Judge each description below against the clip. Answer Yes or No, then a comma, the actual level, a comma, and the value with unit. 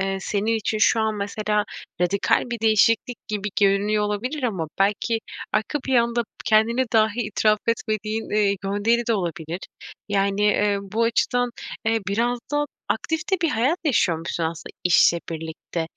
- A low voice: No, high, 215 Hz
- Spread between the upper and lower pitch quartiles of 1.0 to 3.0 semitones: Yes, narrow, 2.6 semitones